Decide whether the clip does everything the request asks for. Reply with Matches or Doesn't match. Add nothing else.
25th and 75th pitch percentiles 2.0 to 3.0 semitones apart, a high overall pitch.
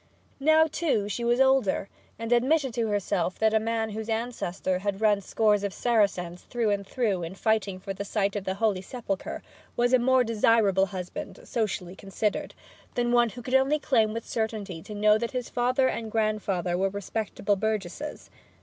Doesn't match